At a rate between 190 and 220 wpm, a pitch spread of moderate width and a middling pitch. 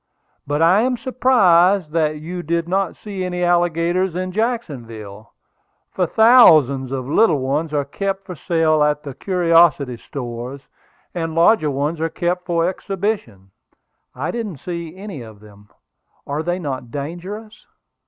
No: average, 150 wpm; average, 4.7 semitones; medium, 165 Hz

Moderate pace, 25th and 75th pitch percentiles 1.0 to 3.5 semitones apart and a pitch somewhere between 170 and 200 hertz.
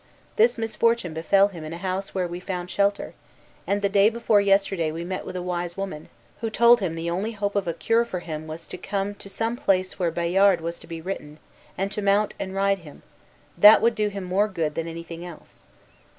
No: fast, 220 wpm; average, 3.1 semitones; high, 190 Hz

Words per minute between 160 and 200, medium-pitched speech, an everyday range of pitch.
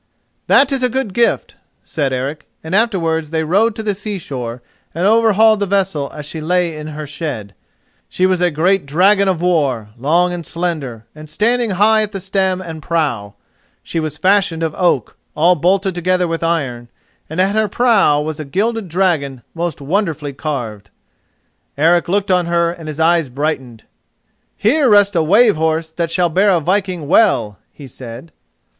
Yes: average, 175 wpm; medium, 170 Hz; average, 4.5 semitones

